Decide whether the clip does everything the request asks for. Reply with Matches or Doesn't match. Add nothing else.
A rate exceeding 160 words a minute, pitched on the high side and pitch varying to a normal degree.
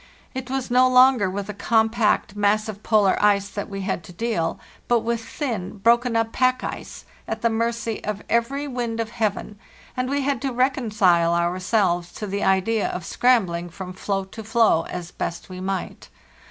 Matches